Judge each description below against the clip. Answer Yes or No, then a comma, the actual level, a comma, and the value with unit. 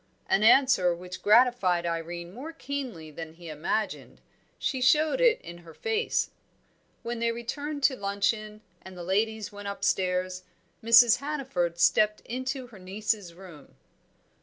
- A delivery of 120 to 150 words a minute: Yes, slow, 135 wpm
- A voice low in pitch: No, high, 210 Hz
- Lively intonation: Yes, wide, 6.0 semitones